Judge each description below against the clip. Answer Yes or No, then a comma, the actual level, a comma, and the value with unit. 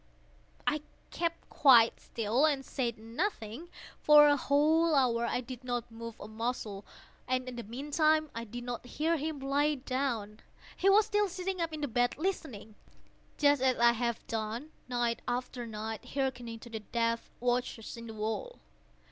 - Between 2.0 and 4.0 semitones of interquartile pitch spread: No, average, 4.4 semitones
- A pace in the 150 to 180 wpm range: Yes, average, 165 wpm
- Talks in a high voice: Yes, very high, 250 Hz